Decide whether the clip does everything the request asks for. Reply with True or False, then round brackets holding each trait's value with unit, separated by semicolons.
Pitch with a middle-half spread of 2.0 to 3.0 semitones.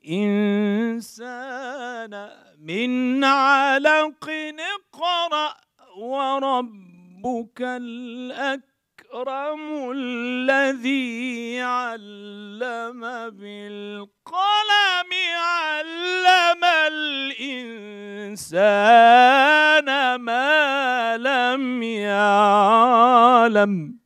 False (3.6 semitones)